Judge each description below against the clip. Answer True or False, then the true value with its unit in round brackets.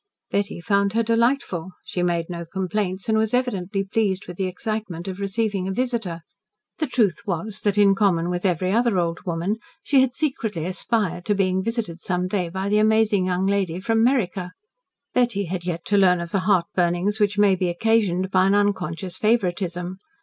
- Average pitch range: True (3.2 semitones)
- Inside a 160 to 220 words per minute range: True (185 wpm)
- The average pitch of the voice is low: False (195 Hz)